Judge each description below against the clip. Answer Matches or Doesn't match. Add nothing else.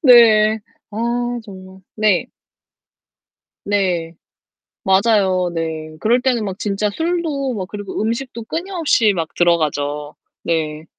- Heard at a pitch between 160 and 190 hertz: Doesn't match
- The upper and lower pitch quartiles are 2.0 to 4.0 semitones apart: Doesn't match